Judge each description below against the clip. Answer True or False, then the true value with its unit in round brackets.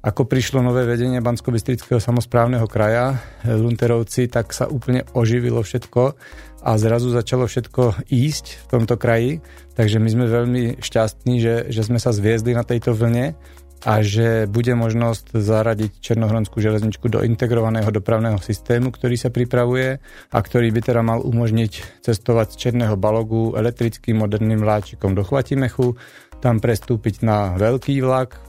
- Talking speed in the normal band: True (145 wpm)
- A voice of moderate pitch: False (115 Hz)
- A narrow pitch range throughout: True (1.8 semitones)